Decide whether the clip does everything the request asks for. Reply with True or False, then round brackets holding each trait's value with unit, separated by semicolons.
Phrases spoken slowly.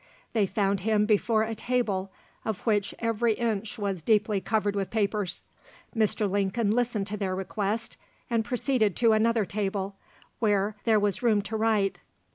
False (155 wpm)